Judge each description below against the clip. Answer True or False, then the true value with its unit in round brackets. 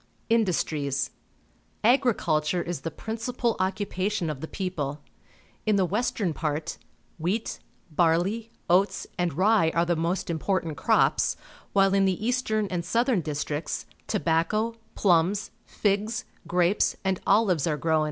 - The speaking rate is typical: False (130 wpm)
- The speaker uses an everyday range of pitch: True (4.7 semitones)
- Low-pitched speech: False (185 Hz)